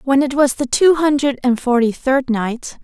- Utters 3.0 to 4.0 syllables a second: No, 4.5 syllables/s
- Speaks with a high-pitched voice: Yes, very high, 265 Hz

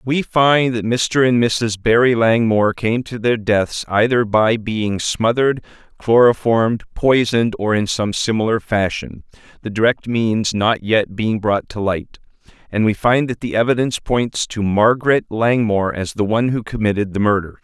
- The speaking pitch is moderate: No, low, 110 Hz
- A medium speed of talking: Yes, average, 165 wpm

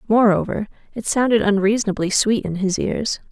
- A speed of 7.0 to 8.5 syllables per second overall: No, 5.4 syllables/s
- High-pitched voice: Yes, high, 210 Hz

